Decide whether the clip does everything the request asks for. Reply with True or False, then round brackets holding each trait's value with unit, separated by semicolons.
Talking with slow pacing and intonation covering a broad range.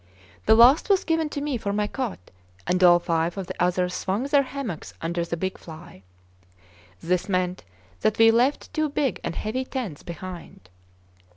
False (175 wpm; 7.0 semitones)